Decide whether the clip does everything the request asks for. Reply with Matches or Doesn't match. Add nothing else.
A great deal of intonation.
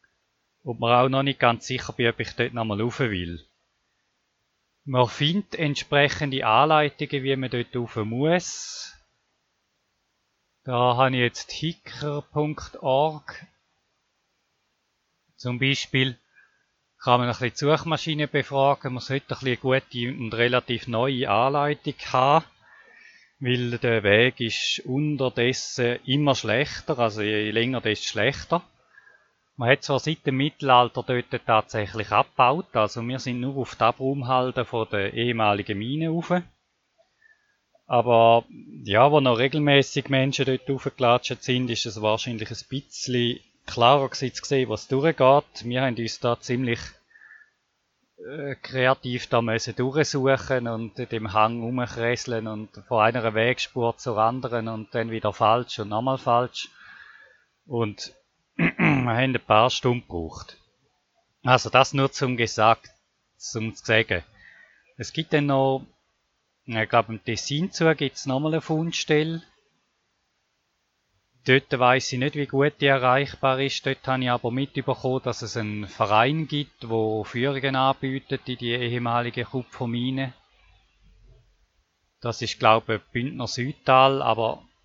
Doesn't match